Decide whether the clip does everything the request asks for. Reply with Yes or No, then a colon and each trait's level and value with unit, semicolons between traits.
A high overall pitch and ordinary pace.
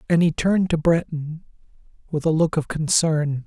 No: medium, 160 Hz; average, 175 wpm